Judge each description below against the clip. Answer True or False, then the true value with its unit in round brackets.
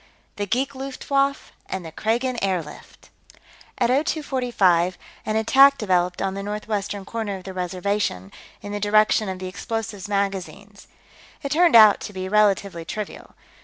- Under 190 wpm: True (145 wpm)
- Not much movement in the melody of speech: False (3.5 semitones)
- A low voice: False (205 Hz)